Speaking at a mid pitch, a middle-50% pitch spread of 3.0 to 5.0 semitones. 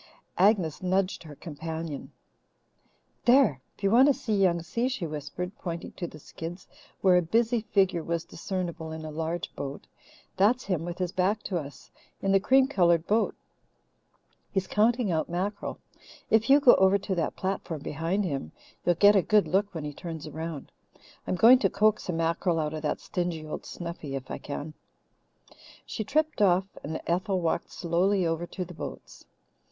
Yes: medium, 180 Hz; average, 3.8 semitones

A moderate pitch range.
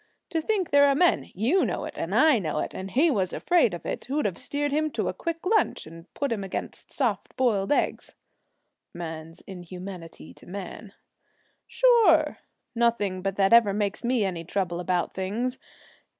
No: wide, 7.7 semitones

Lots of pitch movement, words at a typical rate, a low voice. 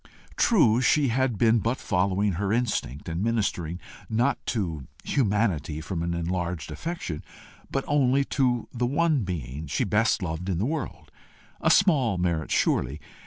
Yes: wide, 6.7 semitones; average, 150 wpm; low, 105 Hz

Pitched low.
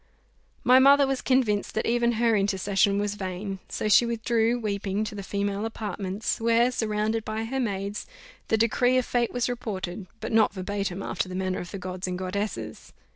No: high, 210 Hz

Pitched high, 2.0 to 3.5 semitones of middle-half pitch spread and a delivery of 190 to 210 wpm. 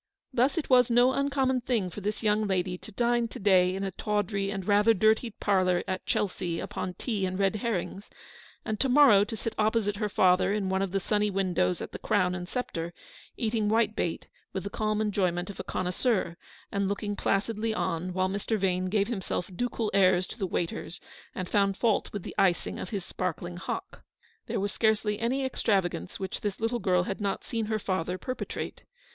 Yes: high, 200 Hz; average, 3.0 semitones; average, 200 wpm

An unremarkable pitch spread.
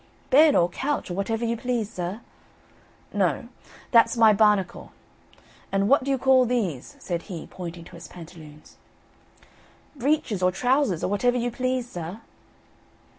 No: wide, 5.9 semitones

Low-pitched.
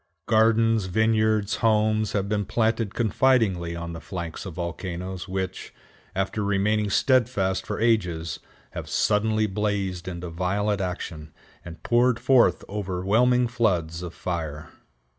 Yes: low, 100 Hz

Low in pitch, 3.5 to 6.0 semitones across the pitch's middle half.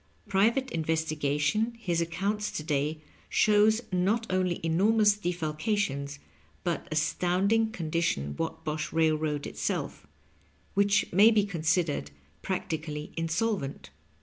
No: medium, 170 Hz; average, 5.0 semitones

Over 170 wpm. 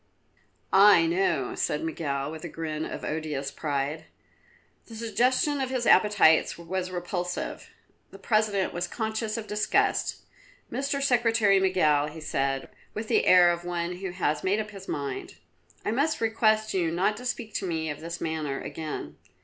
No: average, 160 wpm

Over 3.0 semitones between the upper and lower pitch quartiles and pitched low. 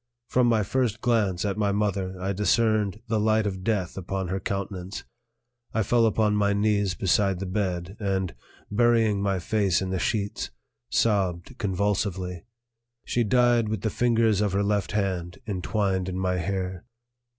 No: narrow, 2.6 semitones; low, 100 Hz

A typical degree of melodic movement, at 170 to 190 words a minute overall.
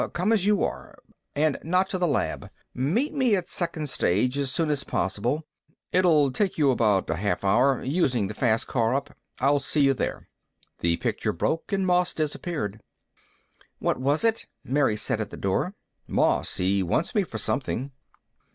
No: wide, 7.0 semitones; average, 175 wpm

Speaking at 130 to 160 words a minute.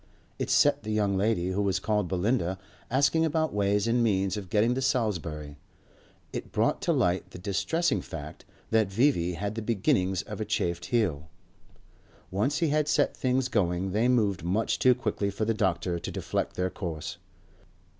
No: average, 175 wpm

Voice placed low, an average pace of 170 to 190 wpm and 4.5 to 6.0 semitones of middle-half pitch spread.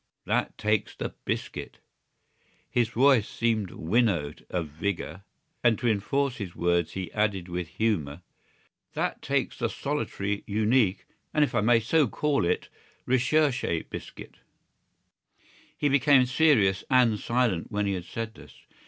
No: low, 110 Hz; slow, 135 wpm; average, 5.3 semitones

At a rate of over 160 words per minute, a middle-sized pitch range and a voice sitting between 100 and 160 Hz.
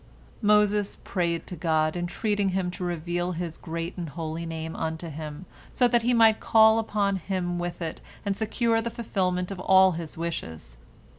No: average, 175 wpm; average, 3.8 semitones; medium, 180 Hz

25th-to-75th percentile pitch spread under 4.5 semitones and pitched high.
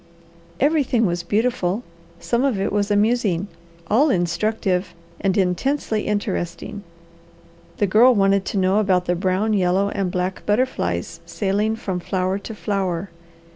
Yes: average, 2.9 semitones; high, 200 Hz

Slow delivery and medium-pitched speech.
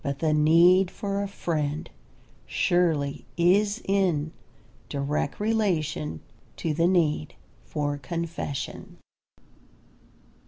Yes: slow, 90 wpm; medium, 165 Hz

